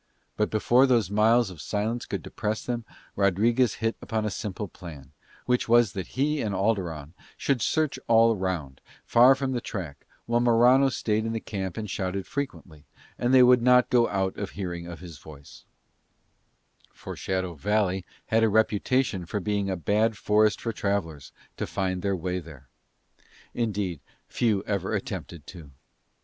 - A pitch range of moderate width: Yes, average, 4.2 semitones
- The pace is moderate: Yes, average, 165 wpm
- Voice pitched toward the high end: No, low, 105 Hz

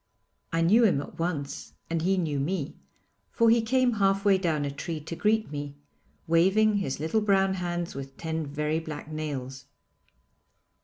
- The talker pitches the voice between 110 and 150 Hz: No, medium, 165 Hz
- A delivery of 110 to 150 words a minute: No, average, 165 wpm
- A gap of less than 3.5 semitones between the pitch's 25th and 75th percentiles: No, average, 4.9 semitones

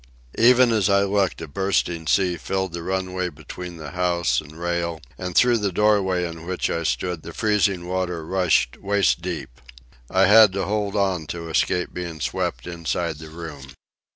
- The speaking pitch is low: Yes, very low, 90 Hz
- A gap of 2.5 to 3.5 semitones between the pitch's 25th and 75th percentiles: Yes, average, 2.8 semitones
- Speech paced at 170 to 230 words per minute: Yes, average, 175 wpm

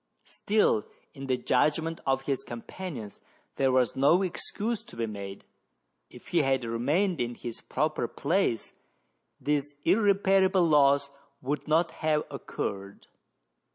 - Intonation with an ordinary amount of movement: No, wide, 5.8 semitones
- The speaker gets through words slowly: Yes, slow, 125 wpm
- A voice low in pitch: No, medium, 145 Hz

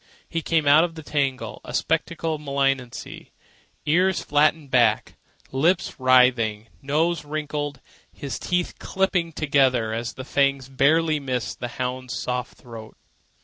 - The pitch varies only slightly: No, average, 3.7 semitones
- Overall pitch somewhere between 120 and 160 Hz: Yes, medium, 140 Hz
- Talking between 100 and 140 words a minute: Yes, slow, 135 wpm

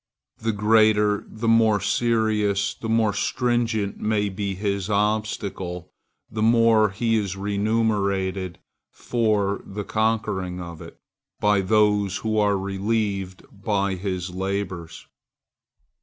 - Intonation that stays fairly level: Yes, narrow, 2.0 semitones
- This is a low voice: Yes, low, 105 Hz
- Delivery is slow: Yes, slow, 110 wpm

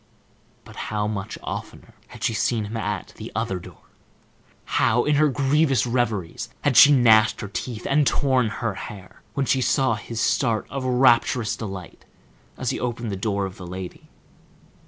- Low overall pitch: Yes, low, 115 Hz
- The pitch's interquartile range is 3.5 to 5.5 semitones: Yes, average, 4.0 semitones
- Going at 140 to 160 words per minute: No, average, 170 wpm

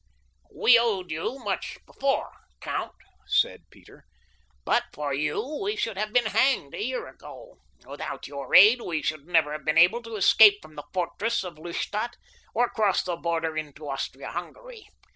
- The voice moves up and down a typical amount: No, wide, 7.1 semitones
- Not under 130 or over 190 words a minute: Yes, average, 160 wpm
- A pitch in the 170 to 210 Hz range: Yes, high, 190 Hz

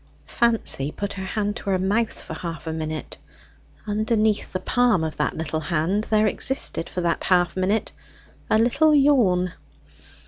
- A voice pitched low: No, high, 195 Hz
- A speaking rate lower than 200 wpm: Yes, average, 160 wpm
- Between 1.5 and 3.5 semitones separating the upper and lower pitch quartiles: No, average, 4.5 semitones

